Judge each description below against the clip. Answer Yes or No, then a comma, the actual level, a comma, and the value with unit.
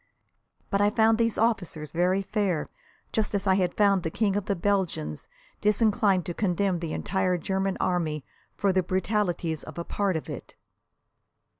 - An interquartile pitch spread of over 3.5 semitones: No, average, 2.7 semitones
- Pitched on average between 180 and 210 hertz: Yes, high, 190 Hz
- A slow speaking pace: No, average, 165 wpm